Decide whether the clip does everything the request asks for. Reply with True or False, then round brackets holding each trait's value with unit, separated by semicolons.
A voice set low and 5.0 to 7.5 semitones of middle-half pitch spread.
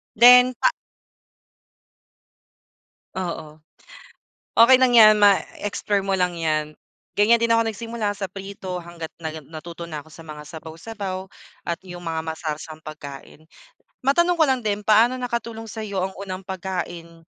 False (190 Hz; 5.3 semitones)